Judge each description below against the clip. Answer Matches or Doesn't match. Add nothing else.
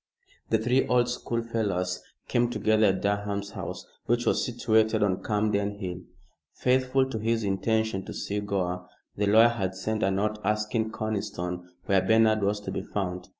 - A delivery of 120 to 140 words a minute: Doesn't match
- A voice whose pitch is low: Matches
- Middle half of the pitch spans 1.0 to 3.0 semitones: Matches